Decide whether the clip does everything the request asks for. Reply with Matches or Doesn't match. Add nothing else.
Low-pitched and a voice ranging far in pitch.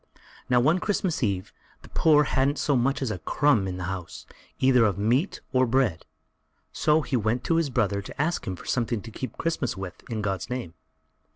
Matches